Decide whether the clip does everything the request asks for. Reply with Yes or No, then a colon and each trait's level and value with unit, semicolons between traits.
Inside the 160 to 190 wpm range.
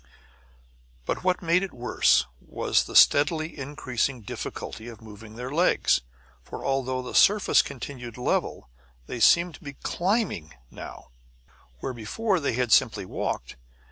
No: average, 140 wpm